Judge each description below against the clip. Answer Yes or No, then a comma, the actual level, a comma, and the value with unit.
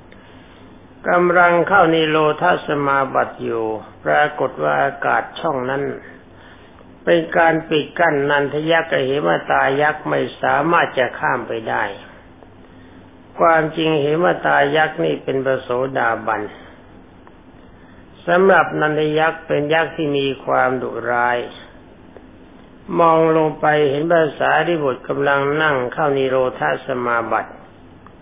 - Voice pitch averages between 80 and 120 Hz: No, medium, 140 Hz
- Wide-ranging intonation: Yes, wide, 9.0 semitones